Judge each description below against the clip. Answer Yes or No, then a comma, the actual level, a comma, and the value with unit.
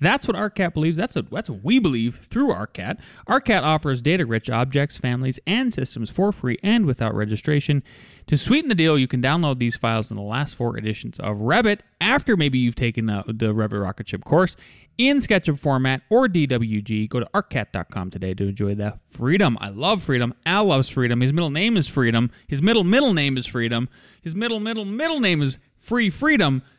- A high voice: No, medium, 140 Hz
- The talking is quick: No, average, 195 wpm